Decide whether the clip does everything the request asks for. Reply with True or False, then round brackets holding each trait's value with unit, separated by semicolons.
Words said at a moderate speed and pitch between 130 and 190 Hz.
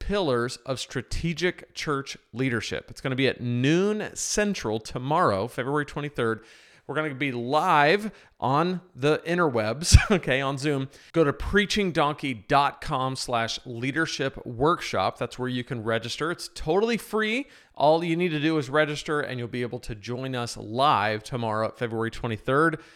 True (145 wpm; 140 Hz)